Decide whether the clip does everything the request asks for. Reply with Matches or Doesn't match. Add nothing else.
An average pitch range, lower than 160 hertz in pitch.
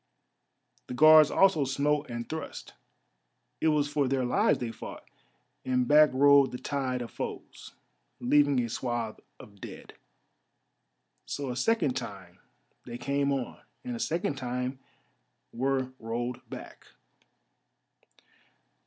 Matches